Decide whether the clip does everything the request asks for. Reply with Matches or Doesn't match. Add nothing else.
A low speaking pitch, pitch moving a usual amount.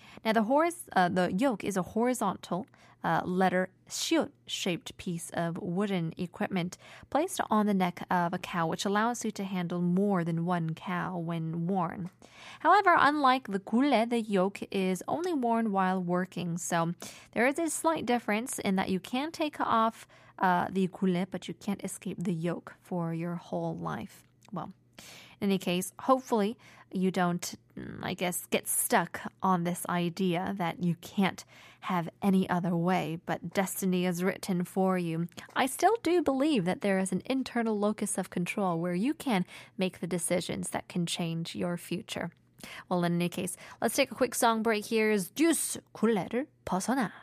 Doesn't match